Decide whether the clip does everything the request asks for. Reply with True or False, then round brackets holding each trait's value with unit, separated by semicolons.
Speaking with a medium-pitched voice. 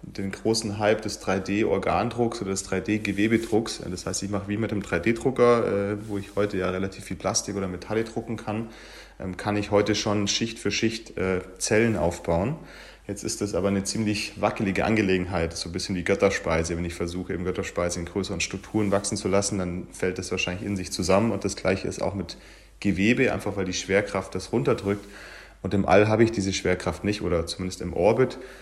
False (100 Hz)